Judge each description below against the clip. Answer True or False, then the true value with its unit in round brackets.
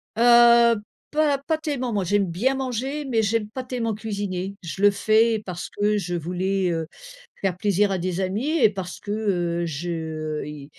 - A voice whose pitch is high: True (205 Hz)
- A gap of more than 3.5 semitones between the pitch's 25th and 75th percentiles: True (4.7 semitones)